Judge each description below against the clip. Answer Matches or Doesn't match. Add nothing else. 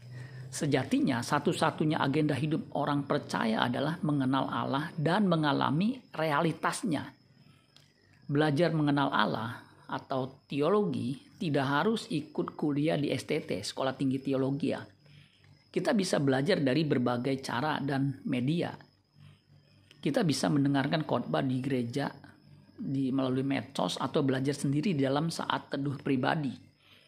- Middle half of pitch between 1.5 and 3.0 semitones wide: Matches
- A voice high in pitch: Doesn't match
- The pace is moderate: Matches